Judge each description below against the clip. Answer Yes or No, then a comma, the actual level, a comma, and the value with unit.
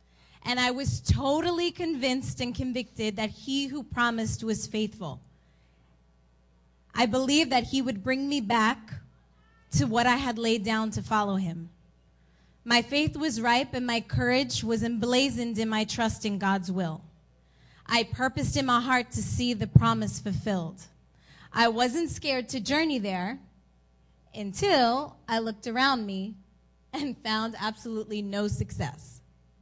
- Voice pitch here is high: Yes, high, 220 Hz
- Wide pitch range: Yes, wide, 7.5 semitones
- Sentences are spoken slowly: No, average, 145 wpm